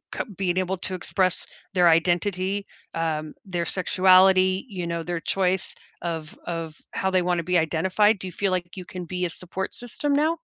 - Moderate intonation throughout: No, narrow, 1.9 semitones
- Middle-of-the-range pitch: Yes, medium, 180 Hz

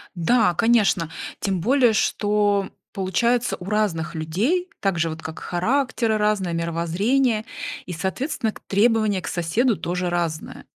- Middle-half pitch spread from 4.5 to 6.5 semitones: Yes, average, 5.0 semitones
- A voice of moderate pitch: No, high, 200 Hz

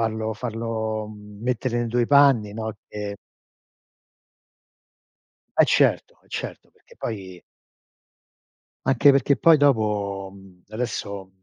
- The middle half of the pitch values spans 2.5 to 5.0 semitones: Yes, average, 2.9 semitones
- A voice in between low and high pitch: No, low, 110 Hz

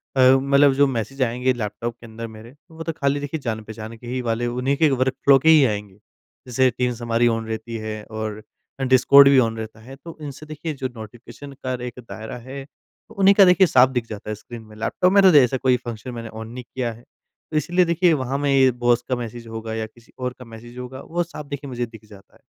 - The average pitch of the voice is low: Yes, low, 125 Hz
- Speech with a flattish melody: No, average, 3.6 semitones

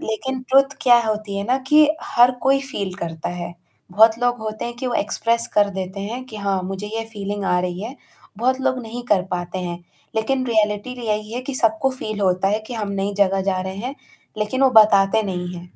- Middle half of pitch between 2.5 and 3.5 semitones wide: No, average, 4.0 semitones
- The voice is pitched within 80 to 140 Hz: No, high, 215 Hz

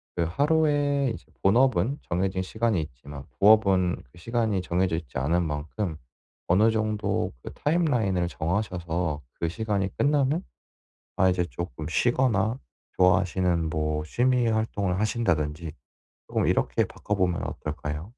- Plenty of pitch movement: No, average, 5.0 semitones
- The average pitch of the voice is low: Yes, very low, 95 Hz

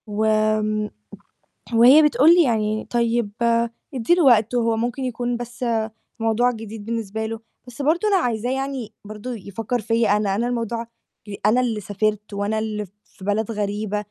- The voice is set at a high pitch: Yes, high, 225 Hz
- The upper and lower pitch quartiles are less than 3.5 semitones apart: Yes, narrow, 2.4 semitones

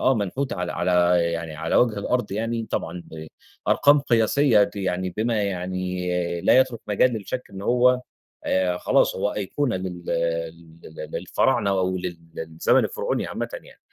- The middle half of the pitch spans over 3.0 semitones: Yes, average, 5.0 semitones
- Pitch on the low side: Yes, low, 100 Hz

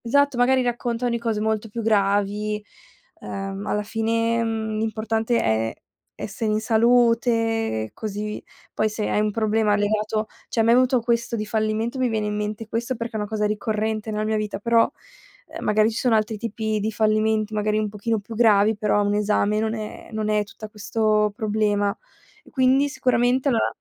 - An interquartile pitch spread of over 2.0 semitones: No, narrow, 1.5 semitones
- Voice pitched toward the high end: Yes, high, 220 Hz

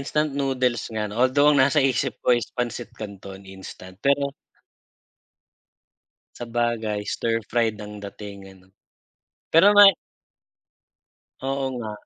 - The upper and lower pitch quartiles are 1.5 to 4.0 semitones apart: No, average, 4.7 semitones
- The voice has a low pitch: Yes, low, 120 Hz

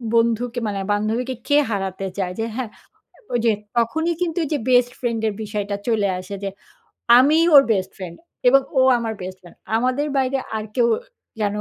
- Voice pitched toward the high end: Yes, high, 230 Hz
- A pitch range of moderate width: Yes, average, 4.0 semitones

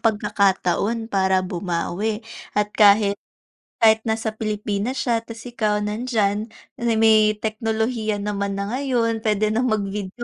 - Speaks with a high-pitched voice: Yes, high, 215 Hz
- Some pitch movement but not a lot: No, narrow, 1.9 semitones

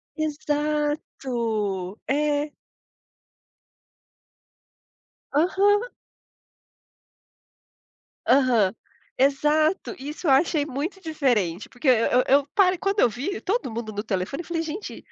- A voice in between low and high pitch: No, very high, 290 Hz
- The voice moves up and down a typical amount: Yes, average, 4.8 semitones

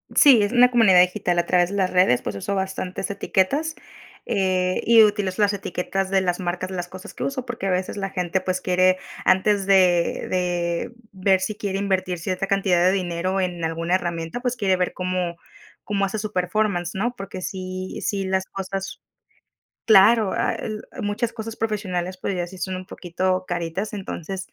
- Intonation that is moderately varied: No, narrow, 1.9 semitones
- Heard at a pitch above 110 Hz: Yes, high, 190 Hz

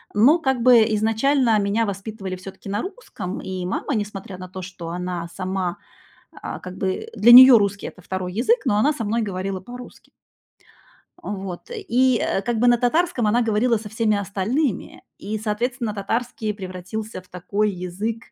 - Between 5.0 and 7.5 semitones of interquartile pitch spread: No, average, 4.1 semitones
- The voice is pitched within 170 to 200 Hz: No, high, 210 Hz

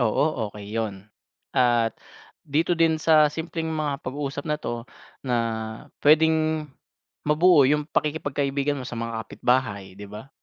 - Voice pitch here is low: No, medium, 145 Hz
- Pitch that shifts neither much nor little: Yes, average, 4.6 semitones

